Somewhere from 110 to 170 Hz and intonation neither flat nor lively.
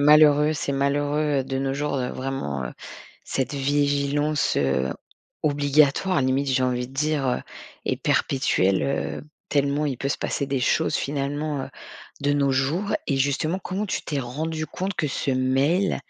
No: medium, 140 Hz; narrow, 1.9 semitones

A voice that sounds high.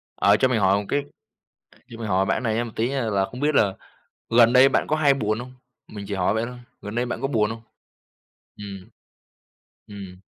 No: low, 115 Hz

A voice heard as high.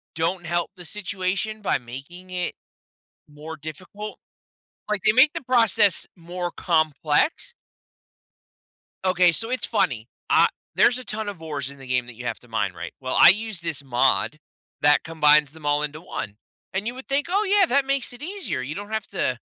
No: medium, 175 Hz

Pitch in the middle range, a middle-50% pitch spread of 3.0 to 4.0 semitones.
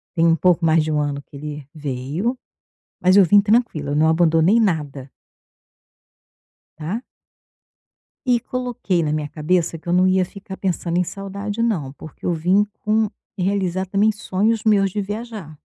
No: medium, 180 Hz; average, 4.7 semitones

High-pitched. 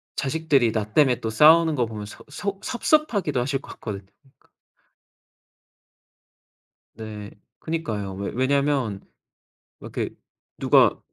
No: low, 130 Hz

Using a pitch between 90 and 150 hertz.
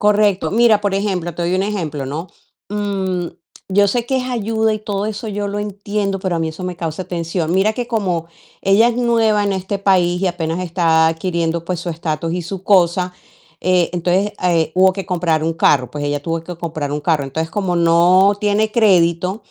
No: medium, 185 Hz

